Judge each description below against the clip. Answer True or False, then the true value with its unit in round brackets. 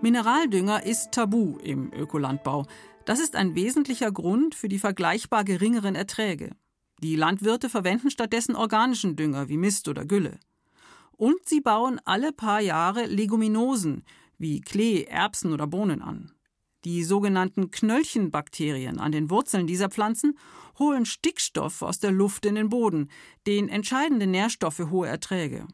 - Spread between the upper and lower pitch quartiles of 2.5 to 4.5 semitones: False (5.0 semitones)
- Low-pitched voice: False (205 Hz)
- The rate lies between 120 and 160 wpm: True (140 wpm)